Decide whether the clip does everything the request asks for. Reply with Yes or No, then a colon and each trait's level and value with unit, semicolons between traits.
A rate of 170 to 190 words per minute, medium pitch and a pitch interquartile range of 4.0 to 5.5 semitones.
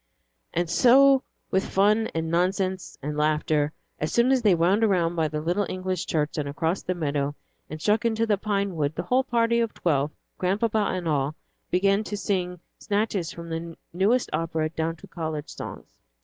Yes: average, 180 wpm; medium, 180 Hz; average, 4.7 semitones